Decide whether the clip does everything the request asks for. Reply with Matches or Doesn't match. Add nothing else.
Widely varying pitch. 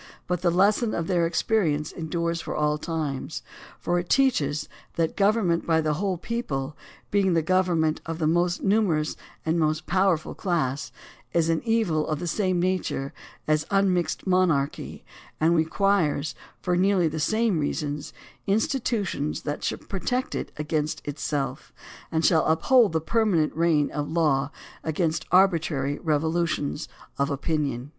Doesn't match